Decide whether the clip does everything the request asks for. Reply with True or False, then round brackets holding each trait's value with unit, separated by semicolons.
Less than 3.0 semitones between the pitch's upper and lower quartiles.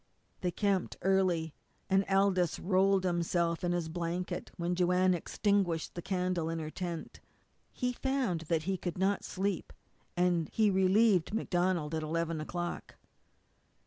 True (2.4 semitones)